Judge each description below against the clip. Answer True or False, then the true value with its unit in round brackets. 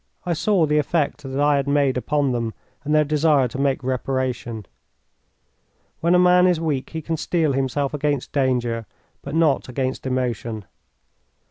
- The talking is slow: False (160 wpm)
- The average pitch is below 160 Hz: True (140 Hz)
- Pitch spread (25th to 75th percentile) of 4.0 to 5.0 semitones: False (2.9 semitones)